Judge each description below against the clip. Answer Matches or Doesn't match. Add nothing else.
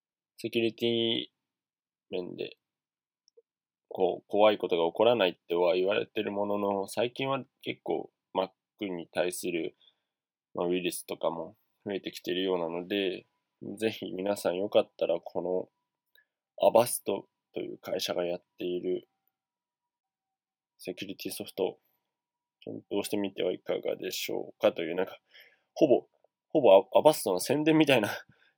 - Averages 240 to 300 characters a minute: Matches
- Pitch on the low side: Matches